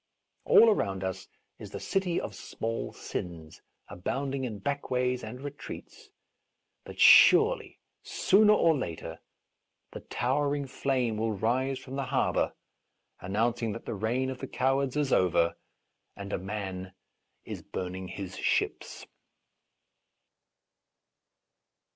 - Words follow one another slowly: Yes, slow, 125 wpm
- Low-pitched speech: Yes, low, 120 Hz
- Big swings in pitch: Yes, wide, 6.0 semitones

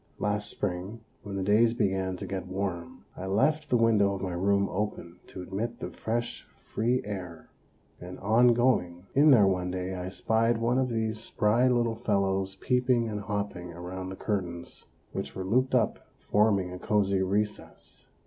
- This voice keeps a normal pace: Yes, average, 170 wpm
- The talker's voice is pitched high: No, low, 100 Hz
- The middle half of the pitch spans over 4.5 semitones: No, average, 3.5 semitones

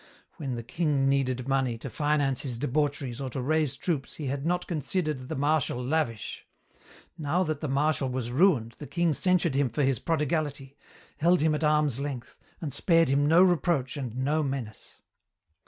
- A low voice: No, medium, 145 Hz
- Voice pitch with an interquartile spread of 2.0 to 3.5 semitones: Yes, average, 3.1 semitones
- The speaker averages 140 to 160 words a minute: No, average, 175 wpm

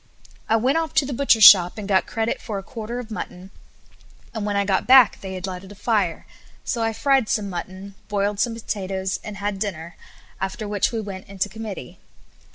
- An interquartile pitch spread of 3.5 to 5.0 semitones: No, average, 2.7 semitones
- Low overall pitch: No, high, 205 Hz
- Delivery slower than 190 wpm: No, average, 200 wpm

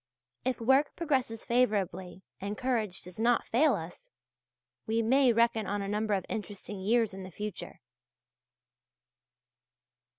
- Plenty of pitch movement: No, average, 3.5 semitones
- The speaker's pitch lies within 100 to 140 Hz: No, high, 220 Hz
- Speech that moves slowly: Yes, slow, 130 wpm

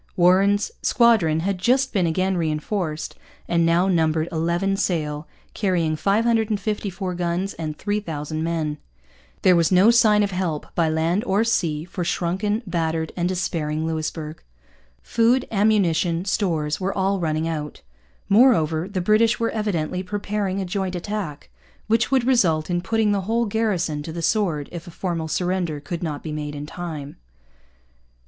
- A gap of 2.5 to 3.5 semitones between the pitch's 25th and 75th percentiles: No, average, 4.2 semitones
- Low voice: No, medium, 180 Hz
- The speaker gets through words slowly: No, average, 150 wpm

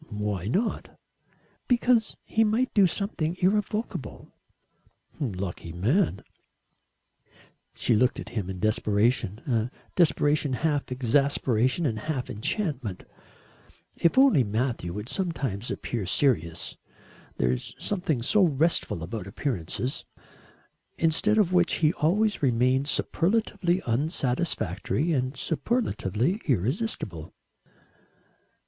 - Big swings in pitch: Yes, wide, 8.6 semitones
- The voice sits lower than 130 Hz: No, low, 135 Hz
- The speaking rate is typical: No, slow, 100 wpm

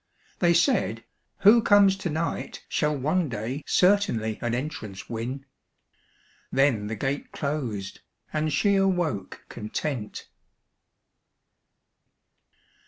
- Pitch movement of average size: No, wide, 7.5 semitones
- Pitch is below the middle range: No, medium, 145 Hz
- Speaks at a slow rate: Yes, slow, 100 wpm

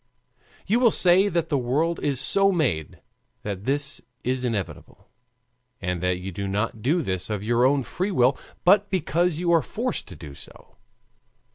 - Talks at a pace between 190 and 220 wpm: No, average, 170 wpm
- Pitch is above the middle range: No, low, 135 Hz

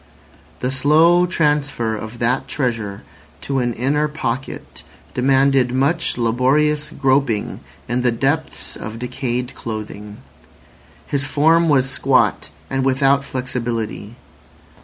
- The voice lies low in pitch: Yes, low, 130 Hz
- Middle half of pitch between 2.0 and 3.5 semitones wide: Yes, average, 3.2 semitones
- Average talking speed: No, slow, 110 wpm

